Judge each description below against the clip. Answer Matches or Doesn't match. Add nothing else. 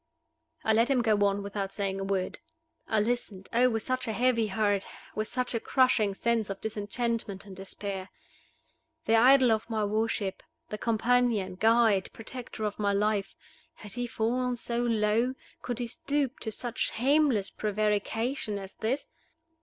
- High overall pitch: Matches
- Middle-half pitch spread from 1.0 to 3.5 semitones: Matches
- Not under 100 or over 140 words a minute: Doesn't match